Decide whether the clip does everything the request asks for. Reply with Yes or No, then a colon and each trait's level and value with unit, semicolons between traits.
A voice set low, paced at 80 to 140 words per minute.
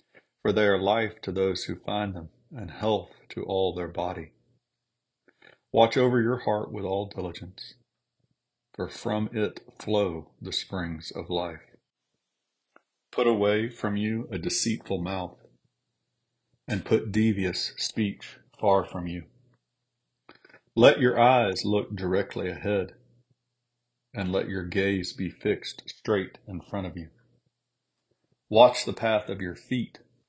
Yes: low, 100 Hz; slow, 135 wpm